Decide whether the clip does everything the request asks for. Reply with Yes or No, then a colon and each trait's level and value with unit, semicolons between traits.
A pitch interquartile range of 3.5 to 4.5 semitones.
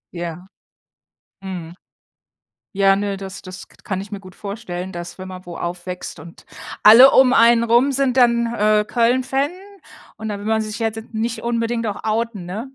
Yes: average, 3.9 semitones